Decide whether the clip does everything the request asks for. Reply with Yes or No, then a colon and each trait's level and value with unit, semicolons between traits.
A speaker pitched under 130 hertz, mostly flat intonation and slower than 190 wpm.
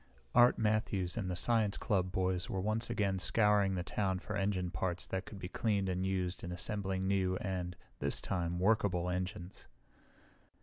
Yes: very low, 95 Hz; narrow, 2.2 semitones; average, 170 wpm